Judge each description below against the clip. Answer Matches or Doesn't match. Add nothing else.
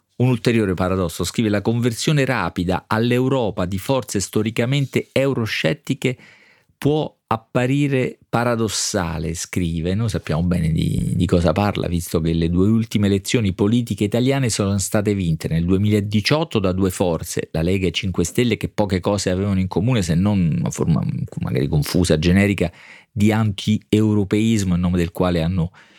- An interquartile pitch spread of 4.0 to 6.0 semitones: Matches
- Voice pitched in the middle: Doesn't match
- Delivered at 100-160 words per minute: Matches